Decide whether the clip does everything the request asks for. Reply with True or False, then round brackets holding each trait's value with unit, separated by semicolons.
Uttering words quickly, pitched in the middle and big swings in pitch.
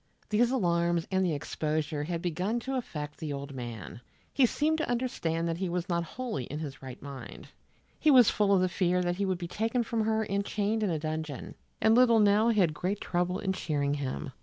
True (215 wpm; 180 Hz; 5.8 semitones)